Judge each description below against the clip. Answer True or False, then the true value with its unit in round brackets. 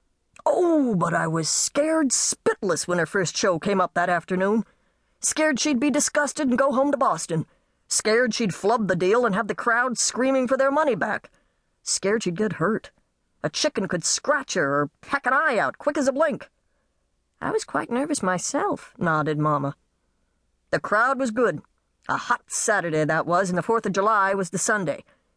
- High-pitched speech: True (215 Hz)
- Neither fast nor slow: True (185 wpm)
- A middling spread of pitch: False (7.4 semitones)